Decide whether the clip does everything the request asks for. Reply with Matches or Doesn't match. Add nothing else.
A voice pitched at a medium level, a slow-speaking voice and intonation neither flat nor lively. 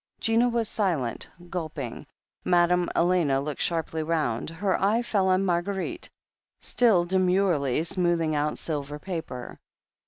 Matches